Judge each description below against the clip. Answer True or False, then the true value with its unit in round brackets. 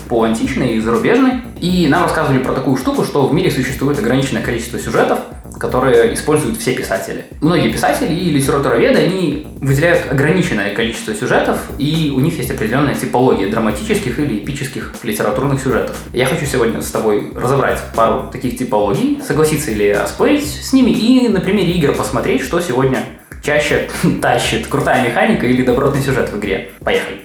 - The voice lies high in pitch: False (140 Hz)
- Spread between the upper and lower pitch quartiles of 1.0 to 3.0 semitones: False (5.2 semitones)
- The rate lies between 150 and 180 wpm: True (160 wpm)